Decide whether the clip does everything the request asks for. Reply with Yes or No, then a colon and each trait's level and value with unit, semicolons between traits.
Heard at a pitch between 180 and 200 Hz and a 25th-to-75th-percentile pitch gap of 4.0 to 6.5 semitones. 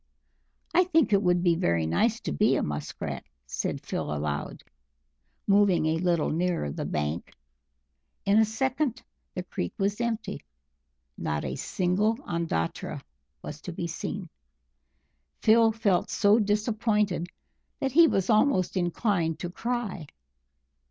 Yes: high, 190 Hz; average, 5.3 semitones